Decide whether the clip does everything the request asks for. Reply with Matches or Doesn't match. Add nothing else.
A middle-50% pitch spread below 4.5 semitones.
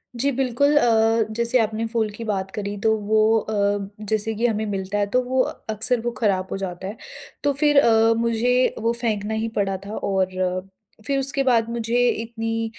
Matches